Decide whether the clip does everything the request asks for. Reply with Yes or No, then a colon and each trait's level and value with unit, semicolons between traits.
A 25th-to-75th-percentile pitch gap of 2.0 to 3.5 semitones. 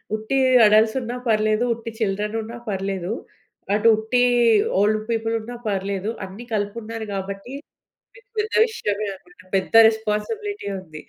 Yes: narrow, 2.5 semitones